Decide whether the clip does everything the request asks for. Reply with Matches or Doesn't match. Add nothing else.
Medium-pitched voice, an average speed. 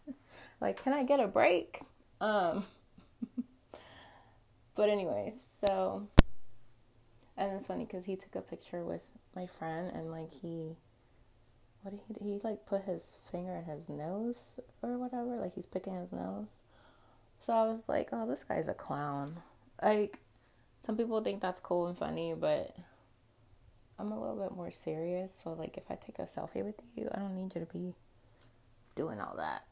Matches